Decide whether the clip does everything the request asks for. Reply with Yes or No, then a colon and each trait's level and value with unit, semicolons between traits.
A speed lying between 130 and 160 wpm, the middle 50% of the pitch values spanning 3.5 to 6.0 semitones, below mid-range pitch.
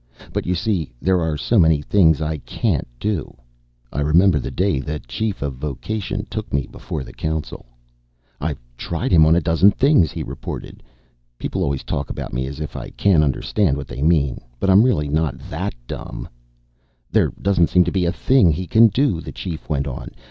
No: average, 195 wpm; average, 4.9 semitones; very low, 80 Hz